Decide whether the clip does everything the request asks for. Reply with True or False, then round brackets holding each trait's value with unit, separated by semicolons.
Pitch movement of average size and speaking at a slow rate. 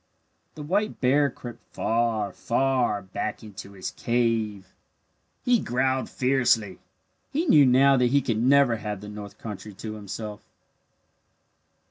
True (4.2 semitones; 130 wpm)